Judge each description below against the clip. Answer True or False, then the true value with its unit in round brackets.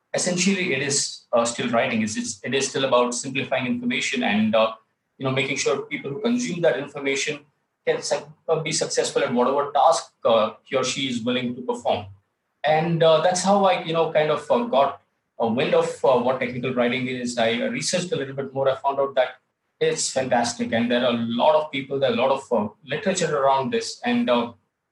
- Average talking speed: False (215 wpm)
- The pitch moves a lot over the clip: True (7.3 semitones)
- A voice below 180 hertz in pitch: True (140 Hz)